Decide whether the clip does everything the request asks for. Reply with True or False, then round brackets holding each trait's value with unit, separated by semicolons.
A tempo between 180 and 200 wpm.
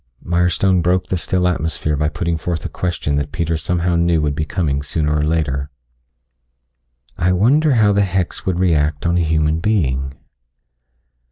False (165 wpm)